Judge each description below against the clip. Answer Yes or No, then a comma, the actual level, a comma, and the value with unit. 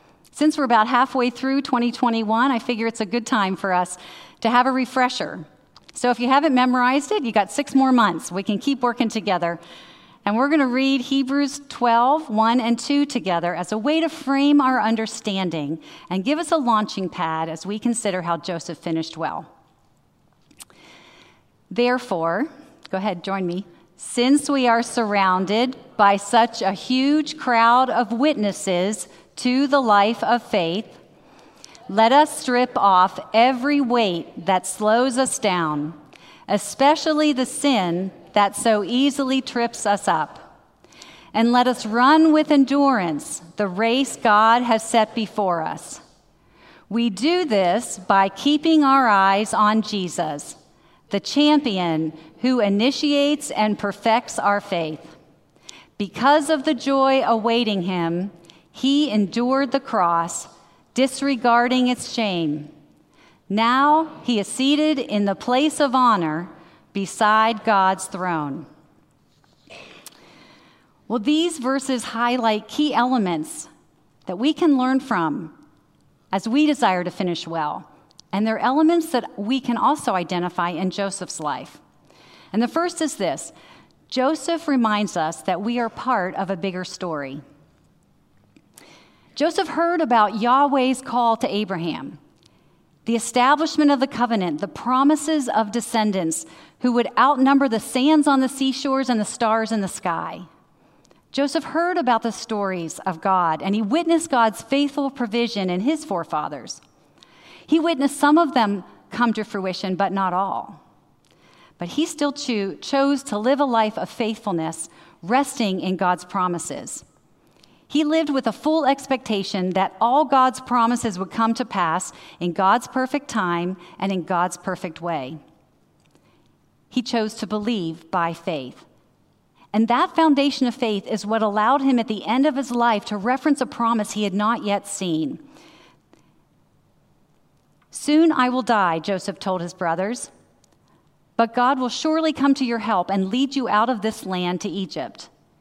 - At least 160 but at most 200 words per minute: No, average, 145 wpm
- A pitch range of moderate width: No, wide, 5.7 semitones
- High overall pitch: Yes, high, 230 Hz